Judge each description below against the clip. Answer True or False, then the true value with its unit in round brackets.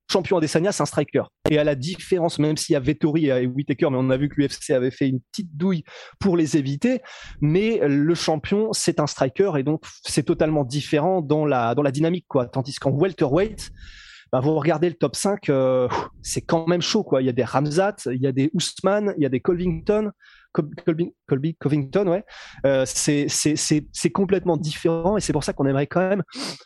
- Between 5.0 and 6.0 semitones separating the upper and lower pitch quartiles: False (4.0 semitones)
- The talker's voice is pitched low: False (155 Hz)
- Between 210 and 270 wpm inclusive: True (220 wpm)